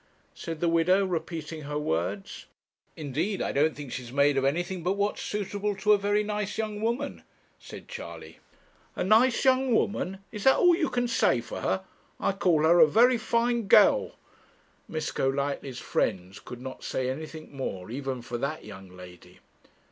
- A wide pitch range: Yes, wide, 7.6 semitones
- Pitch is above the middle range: No, medium, 165 Hz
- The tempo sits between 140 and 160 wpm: No, average, 170 wpm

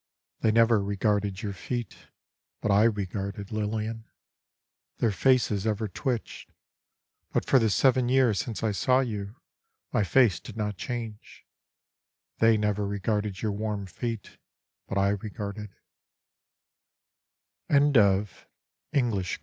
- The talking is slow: Yes, slow, 110 wpm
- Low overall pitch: Yes, low, 105 Hz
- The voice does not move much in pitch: Yes, narrow, 2.2 semitones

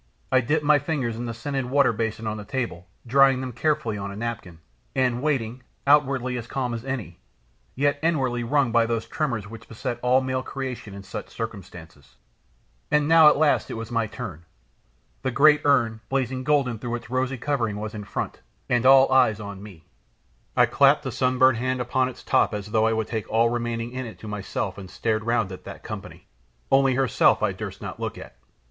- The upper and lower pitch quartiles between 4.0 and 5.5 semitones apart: No, average, 3.2 semitones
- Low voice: Yes, low, 120 Hz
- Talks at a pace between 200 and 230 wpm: Yes, fast, 205 wpm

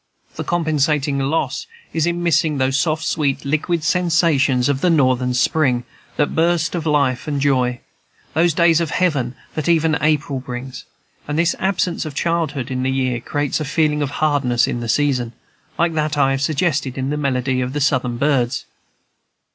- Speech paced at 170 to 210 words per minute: Yes, average, 175 wpm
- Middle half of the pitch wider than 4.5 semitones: No, average, 3.5 semitones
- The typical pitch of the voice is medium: Yes, medium, 145 Hz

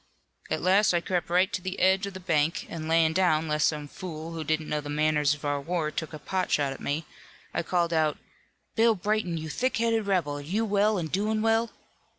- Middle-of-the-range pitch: Yes, medium, 170 Hz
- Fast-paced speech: Yes, fast, 225 wpm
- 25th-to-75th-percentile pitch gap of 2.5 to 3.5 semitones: No, average, 4.1 semitones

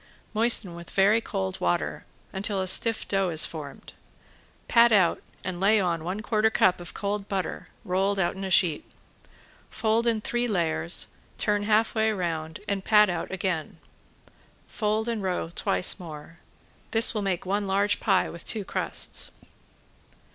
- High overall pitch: Yes, high, 195 Hz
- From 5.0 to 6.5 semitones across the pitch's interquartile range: No, average, 3.5 semitones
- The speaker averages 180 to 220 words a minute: No, average, 155 wpm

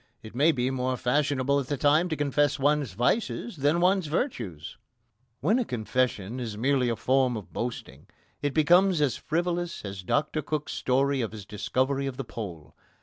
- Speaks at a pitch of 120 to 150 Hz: Yes, low, 135 Hz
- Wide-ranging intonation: No, average, 3.9 semitones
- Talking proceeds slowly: No, average, 175 wpm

